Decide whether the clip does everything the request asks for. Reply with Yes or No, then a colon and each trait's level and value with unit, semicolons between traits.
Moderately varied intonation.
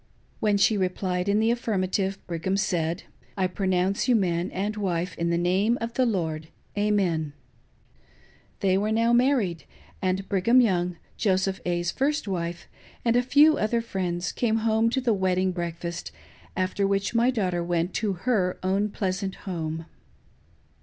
Yes: average, 3.5 semitones